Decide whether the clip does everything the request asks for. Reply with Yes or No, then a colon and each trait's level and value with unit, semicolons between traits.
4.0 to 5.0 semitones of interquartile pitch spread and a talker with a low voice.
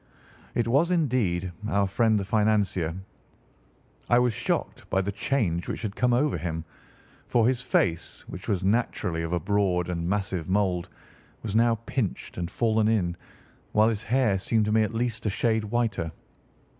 Yes: average, 4.4 semitones; low, 105 Hz